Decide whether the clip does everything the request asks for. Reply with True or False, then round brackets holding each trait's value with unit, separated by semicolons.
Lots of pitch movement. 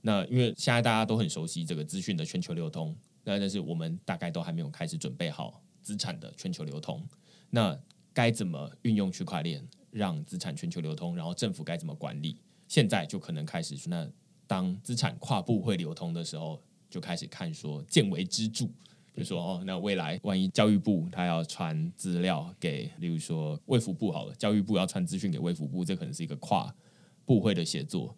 True (8.3 semitones)